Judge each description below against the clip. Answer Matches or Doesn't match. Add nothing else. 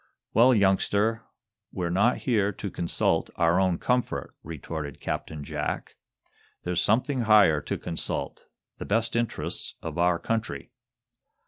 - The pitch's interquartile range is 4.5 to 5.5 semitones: Matches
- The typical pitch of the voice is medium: Doesn't match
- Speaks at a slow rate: Matches